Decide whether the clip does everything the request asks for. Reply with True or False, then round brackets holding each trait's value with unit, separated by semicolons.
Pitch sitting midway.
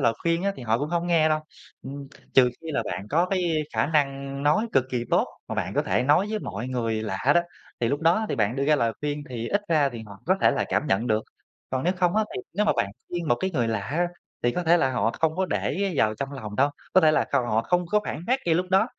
True (145 Hz)